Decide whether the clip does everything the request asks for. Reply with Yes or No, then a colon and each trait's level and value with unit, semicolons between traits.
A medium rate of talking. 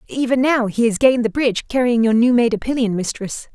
No: fast, 235 wpm